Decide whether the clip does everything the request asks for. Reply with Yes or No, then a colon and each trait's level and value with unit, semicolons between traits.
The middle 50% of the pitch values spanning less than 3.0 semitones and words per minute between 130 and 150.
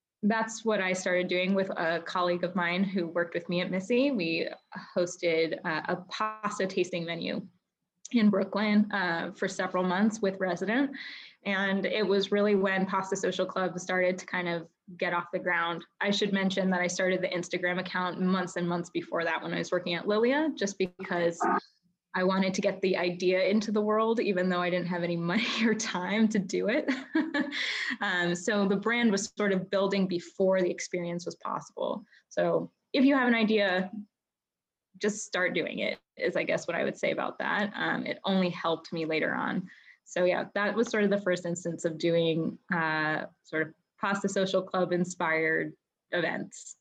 No: narrow, 2.5 semitones; average, 185 wpm